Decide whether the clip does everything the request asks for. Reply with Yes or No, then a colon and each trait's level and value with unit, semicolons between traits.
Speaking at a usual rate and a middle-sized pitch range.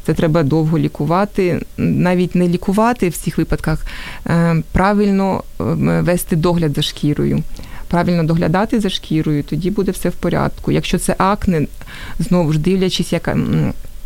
Yes: average, 130 wpm; average, 3.0 semitones